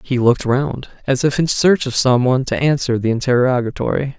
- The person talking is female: No, male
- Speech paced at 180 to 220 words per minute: Yes, average, 200 wpm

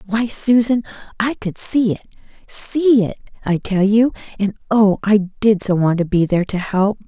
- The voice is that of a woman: Yes, female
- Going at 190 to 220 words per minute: No, average, 180 wpm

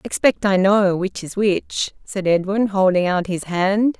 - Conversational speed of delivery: Yes, average, 195 wpm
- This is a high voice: Yes, high, 195 Hz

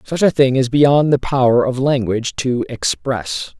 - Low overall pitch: Yes, low, 125 Hz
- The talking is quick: No, average, 185 wpm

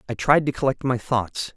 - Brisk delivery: Yes, fast, 230 wpm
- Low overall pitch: Yes, low, 125 Hz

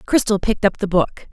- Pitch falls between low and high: No, high, 205 Hz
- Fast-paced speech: Yes, fast, 225 wpm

